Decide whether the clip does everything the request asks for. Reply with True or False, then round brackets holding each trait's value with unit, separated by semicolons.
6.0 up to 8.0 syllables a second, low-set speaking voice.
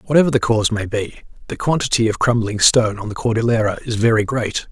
True (6.4 syllables/s; 115 Hz)